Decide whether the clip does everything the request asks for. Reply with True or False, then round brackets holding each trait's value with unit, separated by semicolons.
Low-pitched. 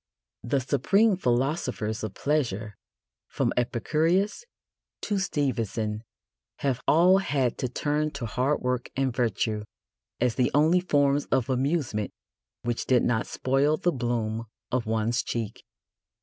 True (130 Hz)